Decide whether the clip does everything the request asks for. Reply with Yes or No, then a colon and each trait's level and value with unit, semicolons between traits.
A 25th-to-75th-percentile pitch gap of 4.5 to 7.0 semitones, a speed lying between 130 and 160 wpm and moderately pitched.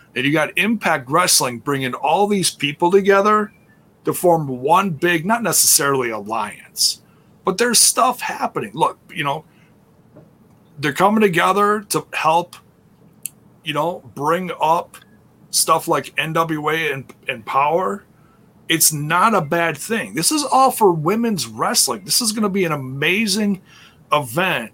Yes: average, 5.2 semitones; average, 140 wpm; medium, 175 Hz